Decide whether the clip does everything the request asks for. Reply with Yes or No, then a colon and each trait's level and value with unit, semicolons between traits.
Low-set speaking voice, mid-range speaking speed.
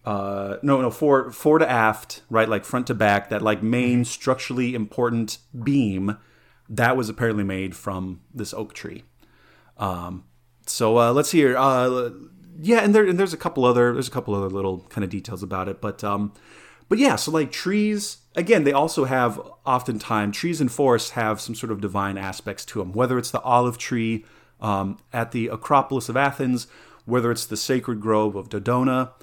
Yes: low, 120 Hz; average, 190 wpm